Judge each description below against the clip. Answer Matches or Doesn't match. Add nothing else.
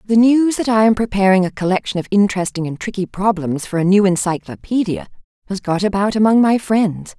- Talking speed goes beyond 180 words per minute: Matches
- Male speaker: Doesn't match